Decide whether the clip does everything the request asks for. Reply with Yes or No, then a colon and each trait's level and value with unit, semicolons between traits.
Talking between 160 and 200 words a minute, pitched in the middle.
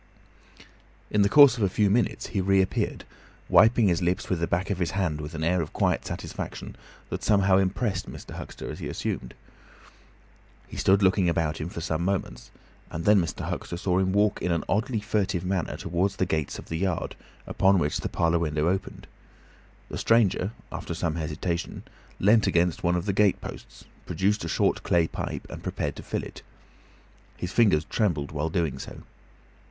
No: average, 185 wpm; very low, 90 Hz